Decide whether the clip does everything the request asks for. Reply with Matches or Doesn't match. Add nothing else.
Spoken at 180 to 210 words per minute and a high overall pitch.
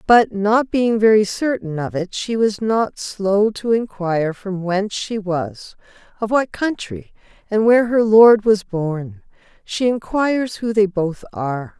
Doesn't match